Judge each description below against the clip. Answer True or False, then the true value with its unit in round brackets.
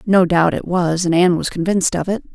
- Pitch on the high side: False (180 Hz)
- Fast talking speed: True (255 wpm)